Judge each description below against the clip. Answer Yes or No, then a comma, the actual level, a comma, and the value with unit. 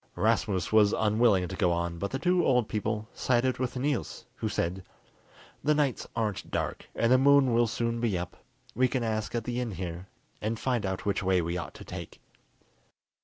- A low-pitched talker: Yes, low, 110 Hz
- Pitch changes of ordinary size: Yes, average, 4.7 semitones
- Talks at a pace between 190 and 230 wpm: Yes, average, 195 wpm